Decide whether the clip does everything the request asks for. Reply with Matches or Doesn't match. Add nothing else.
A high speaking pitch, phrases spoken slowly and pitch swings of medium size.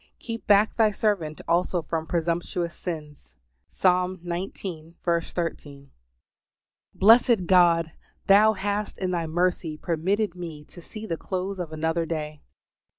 Doesn't match